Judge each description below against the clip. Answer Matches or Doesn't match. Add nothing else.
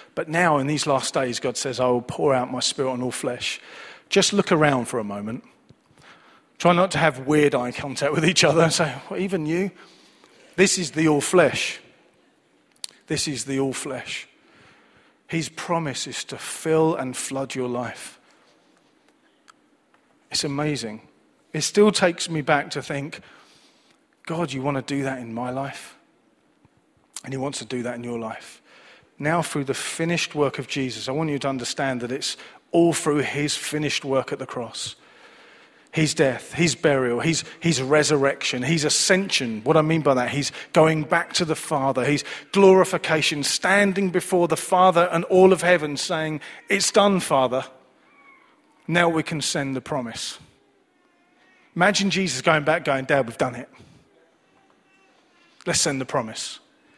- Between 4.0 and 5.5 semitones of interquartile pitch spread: Matches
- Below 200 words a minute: Matches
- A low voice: Doesn't match